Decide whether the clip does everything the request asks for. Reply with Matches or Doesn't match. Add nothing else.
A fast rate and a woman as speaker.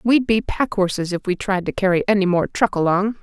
Matches